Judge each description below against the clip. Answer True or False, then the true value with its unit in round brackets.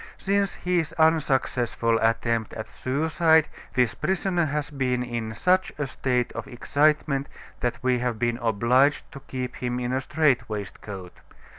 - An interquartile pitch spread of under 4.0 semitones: False (4.5 semitones)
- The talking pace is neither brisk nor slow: True (145 wpm)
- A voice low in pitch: True (130 Hz)